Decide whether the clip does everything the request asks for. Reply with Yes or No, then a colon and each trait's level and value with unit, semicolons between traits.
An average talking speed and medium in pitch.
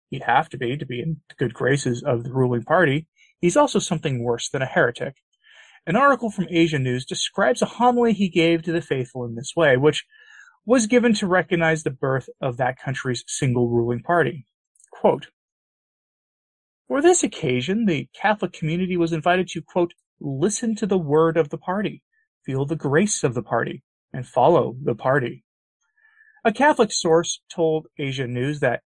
Yes: average, 175 wpm; medium, 165 Hz